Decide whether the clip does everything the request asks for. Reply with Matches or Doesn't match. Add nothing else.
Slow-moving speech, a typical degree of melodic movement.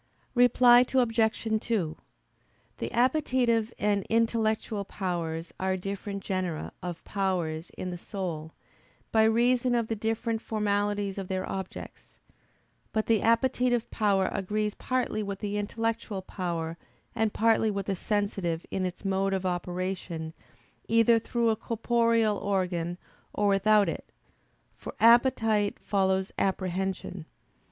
Matches